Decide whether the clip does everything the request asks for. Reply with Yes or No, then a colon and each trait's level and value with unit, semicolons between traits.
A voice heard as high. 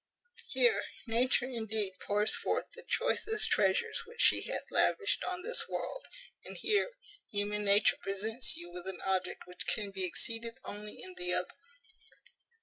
Yes: high, 220 Hz